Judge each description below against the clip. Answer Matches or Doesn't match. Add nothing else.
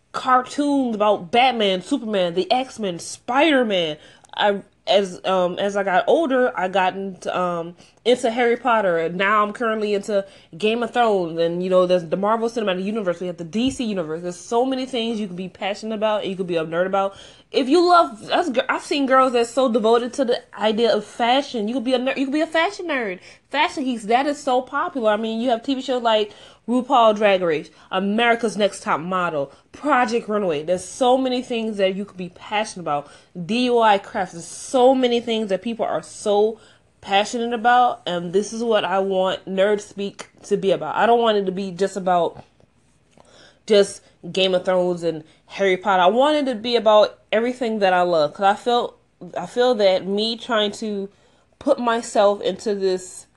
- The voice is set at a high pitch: Matches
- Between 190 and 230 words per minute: Matches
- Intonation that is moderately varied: Matches